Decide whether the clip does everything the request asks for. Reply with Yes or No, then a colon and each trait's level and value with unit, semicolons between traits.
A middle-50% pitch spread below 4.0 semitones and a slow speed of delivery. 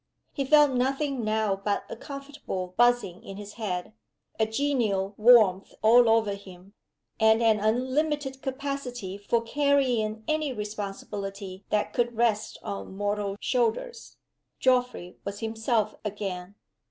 No: average, 4.3 semitones; slow, 125 wpm